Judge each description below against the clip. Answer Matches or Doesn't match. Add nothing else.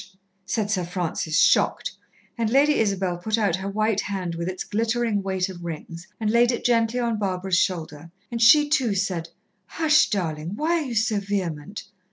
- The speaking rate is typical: Matches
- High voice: Matches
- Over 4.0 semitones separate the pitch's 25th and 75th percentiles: Matches